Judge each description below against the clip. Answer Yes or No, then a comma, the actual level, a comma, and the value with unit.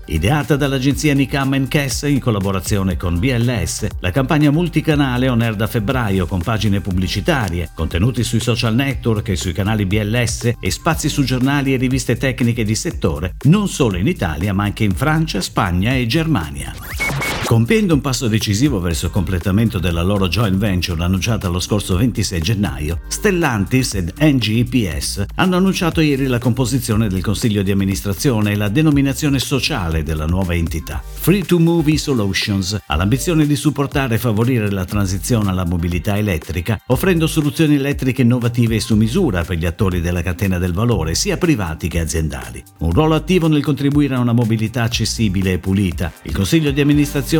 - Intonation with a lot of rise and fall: Yes, wide, 6.5 semitones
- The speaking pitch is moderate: No, low, 115 Hz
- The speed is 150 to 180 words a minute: Yes, average, 165 wpm